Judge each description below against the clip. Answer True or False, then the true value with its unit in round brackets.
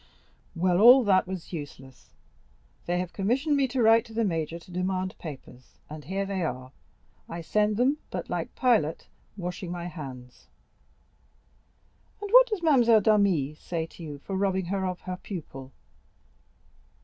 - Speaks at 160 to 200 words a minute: False (150 wpm)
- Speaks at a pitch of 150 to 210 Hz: True (185 Hz)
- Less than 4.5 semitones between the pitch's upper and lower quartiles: False (5.2 semitones)